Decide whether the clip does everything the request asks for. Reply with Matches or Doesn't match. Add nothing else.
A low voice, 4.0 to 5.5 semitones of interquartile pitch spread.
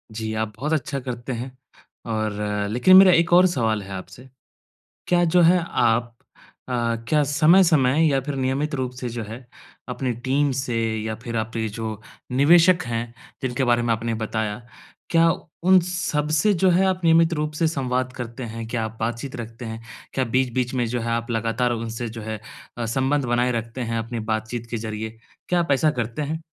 Matches